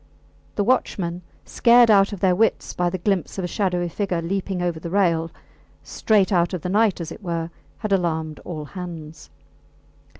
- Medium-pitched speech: Yes, medium, 180 Hz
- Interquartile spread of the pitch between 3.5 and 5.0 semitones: No, average, 2.8 semitones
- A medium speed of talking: Yes, average, 175 wpm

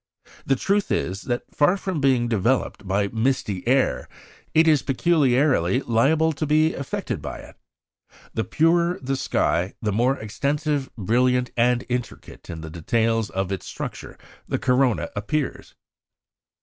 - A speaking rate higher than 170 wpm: No, average, 140 wpm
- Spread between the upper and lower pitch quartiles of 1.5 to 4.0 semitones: No, average, 5.0 semitones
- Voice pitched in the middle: No, low, 125 Hz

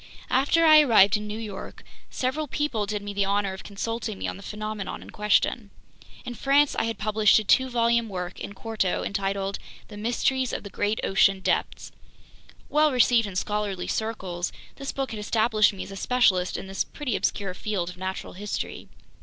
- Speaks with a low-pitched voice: No, high, 210 Hz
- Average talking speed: Yes, average, 185 wpm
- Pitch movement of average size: Yes, average, 3.2 semitones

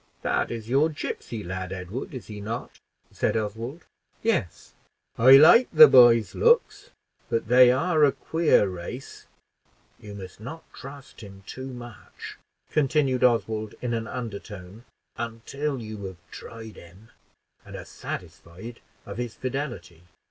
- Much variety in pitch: No, average, 4.5 semitones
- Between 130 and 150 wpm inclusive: Yes, slow, 135 wpm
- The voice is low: Yes, low, 115 Hz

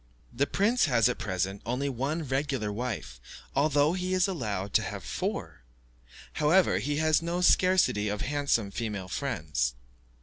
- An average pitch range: No, wide, 7.1 semitones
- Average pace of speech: Yes, average, 145 wpm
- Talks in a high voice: No, low, 135 Hz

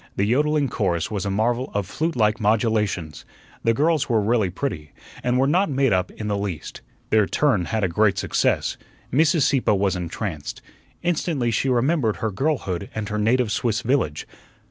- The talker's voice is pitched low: Yes, low, 110 Hz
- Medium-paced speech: Yes, average, 175 wpm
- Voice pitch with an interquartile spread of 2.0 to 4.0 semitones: No, average, 5.2 semitones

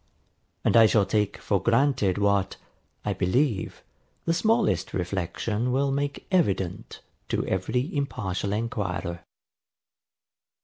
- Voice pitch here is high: No, low, 110 Hz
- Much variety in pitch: Yes, wide, 6.1 semitones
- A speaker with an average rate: No, slow, 105 wpm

